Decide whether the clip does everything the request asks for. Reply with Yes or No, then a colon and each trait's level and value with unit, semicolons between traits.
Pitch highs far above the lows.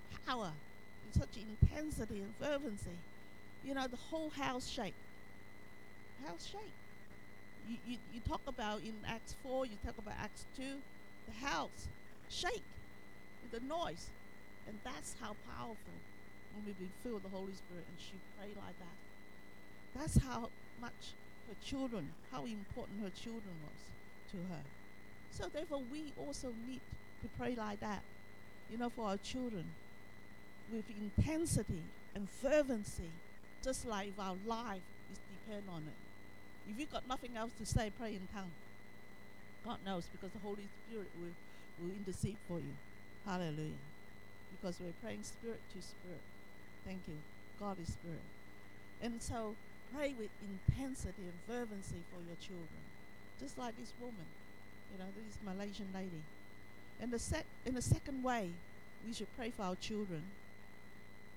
Yes: wide, 5.9 semitones